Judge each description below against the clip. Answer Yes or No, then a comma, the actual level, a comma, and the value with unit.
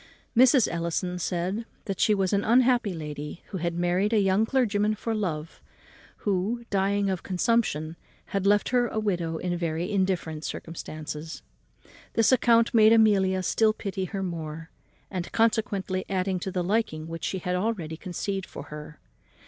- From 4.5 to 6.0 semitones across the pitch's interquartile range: No, average, 4.0 semitones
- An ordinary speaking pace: Yes, average, 160 wpm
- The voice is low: No, high, 190 Hz